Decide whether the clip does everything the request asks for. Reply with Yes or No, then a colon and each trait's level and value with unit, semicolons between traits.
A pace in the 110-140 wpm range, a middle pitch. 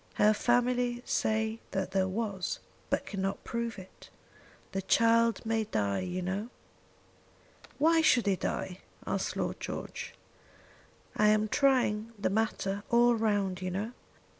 No: slow, 135 wpm; high, 215 Hz